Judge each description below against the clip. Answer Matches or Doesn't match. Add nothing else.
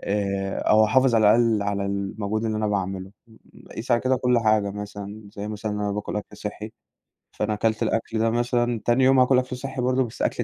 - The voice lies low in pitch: Matches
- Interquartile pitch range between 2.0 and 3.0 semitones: Matches